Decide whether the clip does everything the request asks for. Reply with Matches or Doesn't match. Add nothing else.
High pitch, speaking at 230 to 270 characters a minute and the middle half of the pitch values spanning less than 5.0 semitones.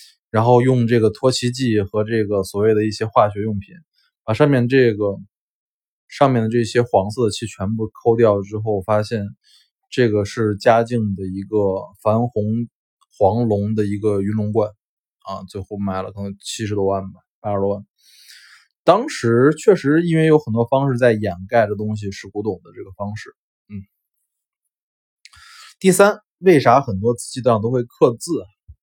Doesn't match